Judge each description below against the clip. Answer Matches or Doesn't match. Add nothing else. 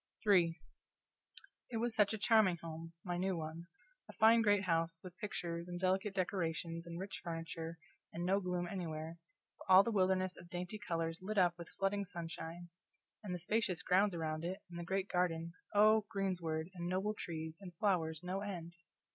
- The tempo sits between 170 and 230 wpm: Matches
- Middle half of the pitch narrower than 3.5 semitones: Matches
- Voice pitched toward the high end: Doesn't match